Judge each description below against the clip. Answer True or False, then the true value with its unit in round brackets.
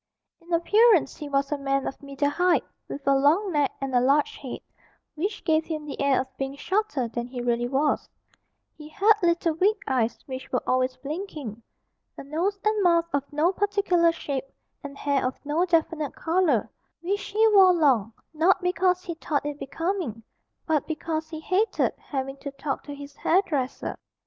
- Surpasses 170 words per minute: True (180 wpm)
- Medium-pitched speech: False (300 Hz)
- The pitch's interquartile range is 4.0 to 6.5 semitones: True (4.6 semitones)